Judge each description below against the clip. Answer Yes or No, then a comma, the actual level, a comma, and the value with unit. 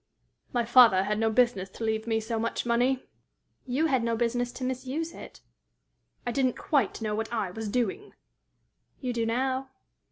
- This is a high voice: Yes, high, 235 Hz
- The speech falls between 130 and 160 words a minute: No, average, 170 wpm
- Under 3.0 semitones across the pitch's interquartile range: Yes, narrow, 2.6 semitones